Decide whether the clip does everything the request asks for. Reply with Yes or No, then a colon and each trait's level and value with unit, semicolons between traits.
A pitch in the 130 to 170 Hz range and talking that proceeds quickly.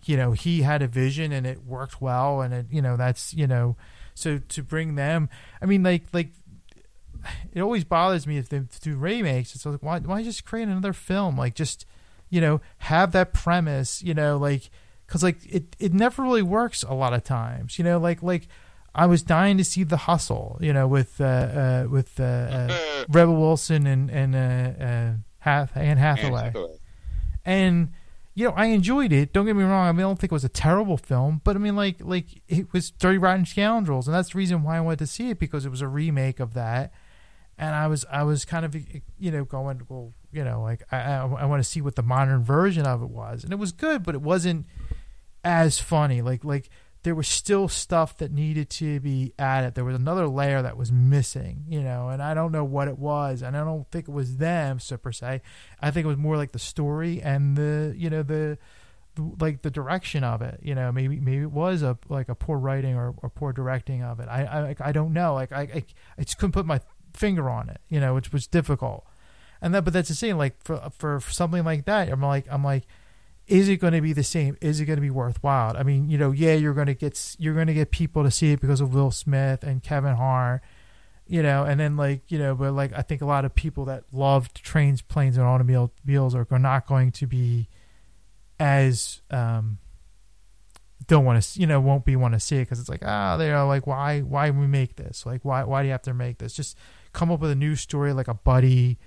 Yes: medium, 140 Hz; fast, 235 wpm